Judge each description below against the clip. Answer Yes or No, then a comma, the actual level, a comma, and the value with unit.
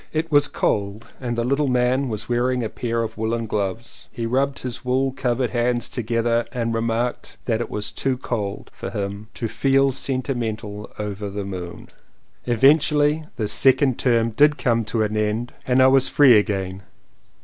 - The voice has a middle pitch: No, low, 120 Hz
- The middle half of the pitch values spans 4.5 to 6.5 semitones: No, average, 3.4 semitones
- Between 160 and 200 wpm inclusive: Yes, average, 170 wpm